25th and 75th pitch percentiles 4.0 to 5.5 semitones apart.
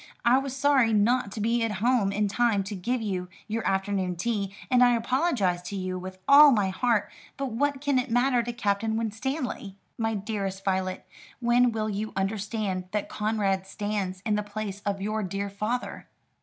No: average, 3.5 semitones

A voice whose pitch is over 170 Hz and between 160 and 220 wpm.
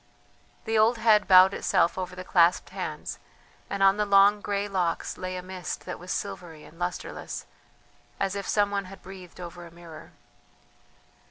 Yes: medium, 185 Hz; average, 170 wpm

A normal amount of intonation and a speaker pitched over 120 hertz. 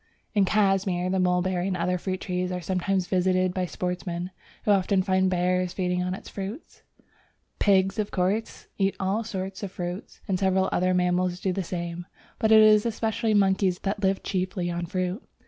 No: narrow, 1.5 semitones; medium, 185 Hz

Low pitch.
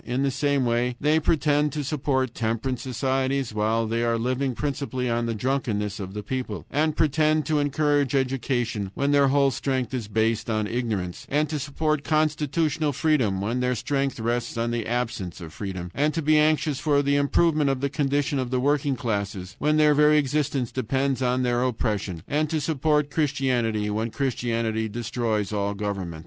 Yes: low, 130 Hz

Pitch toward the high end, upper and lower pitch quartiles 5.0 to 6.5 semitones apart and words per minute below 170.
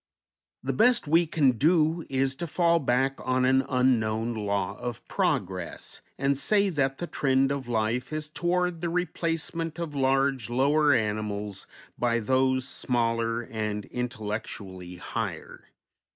No: low, 130 Hz; average, 5.3 semitones; slow, 135 wpm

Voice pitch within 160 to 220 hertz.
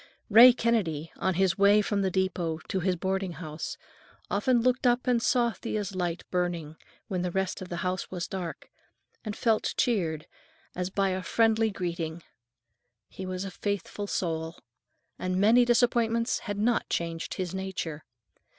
Yes: high, 190 Hz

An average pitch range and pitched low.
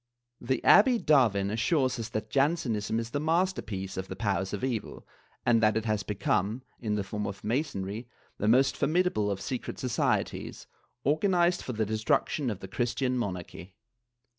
Yes: average, 4.9 semitones; low, 115 Hz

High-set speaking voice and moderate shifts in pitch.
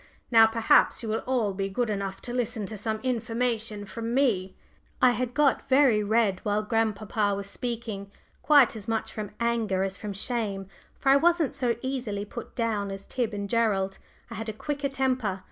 Yes: high, 225 Hz; average, 3.3 semitones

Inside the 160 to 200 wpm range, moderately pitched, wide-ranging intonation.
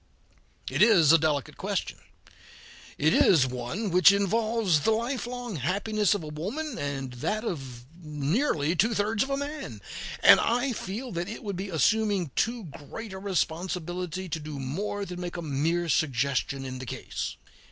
Yes: average, 165 wpm; medium, 180 Hz; wide, 6.4 semitones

